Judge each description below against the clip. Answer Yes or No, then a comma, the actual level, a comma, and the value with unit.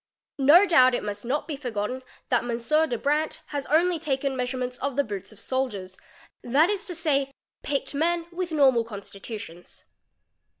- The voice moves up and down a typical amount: Yes, average, 4.6 semitones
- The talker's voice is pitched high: Yes, very high, 270 Hz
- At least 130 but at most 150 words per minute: No, average, 165 wpm